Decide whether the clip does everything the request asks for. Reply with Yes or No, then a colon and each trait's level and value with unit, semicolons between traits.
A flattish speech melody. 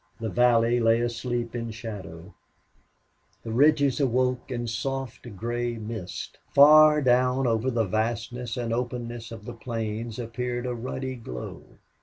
Yes: narrow, 1.8 semitones